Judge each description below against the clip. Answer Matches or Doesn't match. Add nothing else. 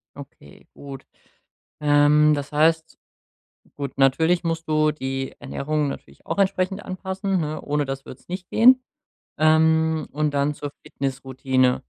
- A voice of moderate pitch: Matches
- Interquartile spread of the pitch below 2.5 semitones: Doesn't match